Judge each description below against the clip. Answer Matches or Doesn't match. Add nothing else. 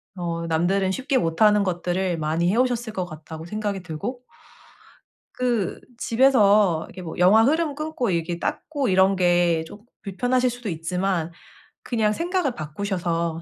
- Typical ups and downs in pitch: Doesn't match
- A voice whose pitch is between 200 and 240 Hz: Doesn't match